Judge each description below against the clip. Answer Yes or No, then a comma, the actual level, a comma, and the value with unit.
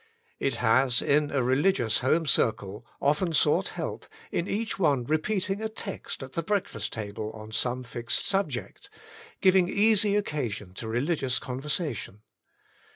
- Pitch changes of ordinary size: No, wide, 7.7 semitones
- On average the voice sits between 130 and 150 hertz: Yes, medium, 140 Hz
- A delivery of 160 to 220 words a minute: No, average, 140 wpm